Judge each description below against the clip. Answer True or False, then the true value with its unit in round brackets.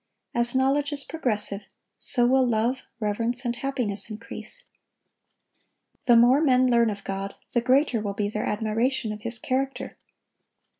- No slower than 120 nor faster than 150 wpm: True (145 wpm)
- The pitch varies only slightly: False (3.5 semitones)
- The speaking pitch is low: False (240 Hz)